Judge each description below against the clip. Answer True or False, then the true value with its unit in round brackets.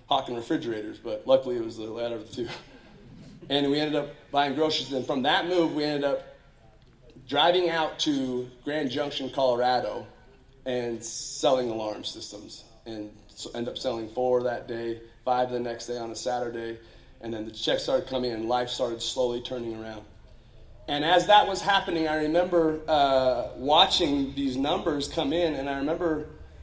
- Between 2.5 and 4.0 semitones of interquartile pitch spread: False (4.5 semitones)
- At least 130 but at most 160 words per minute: False (175 wpm)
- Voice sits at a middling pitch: False (130 Hz)